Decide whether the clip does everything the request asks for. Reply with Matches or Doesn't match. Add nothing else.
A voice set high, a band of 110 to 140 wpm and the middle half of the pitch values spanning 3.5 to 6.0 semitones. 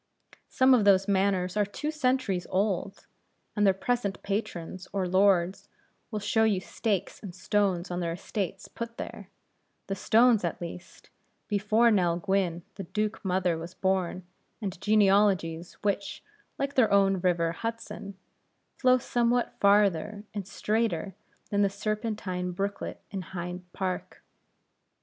Doesn't match